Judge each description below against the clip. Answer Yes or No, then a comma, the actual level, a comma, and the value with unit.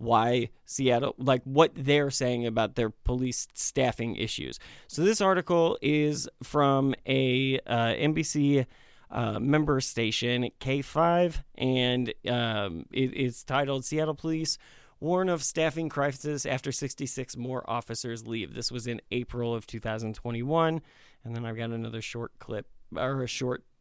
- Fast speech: No, slow, 135 wpm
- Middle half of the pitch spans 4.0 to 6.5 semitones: No, average, 3.6 semitones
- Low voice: Yes, low, 130 Hz